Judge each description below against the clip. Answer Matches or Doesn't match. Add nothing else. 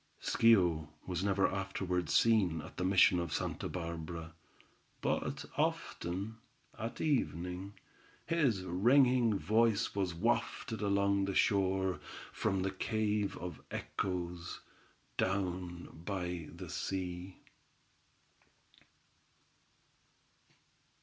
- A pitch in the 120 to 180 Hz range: Doesn't match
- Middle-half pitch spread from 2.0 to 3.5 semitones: Matches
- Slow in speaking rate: Matches